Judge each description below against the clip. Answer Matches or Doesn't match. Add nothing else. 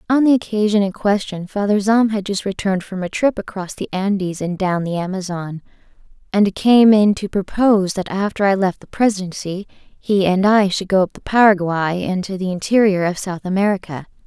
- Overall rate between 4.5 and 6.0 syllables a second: Matches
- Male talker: Doesn't match